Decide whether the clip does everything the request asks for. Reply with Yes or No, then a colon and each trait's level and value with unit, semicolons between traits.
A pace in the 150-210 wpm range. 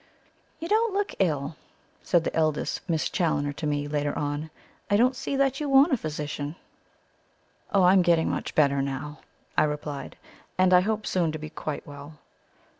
Yes: average, 180 wpm